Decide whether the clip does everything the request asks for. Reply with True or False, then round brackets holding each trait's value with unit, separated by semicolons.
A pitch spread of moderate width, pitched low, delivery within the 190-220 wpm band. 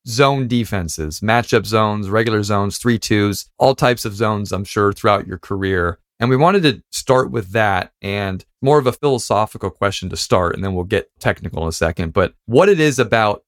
True (4.0 semitones; 105 Hz; 200 wpm)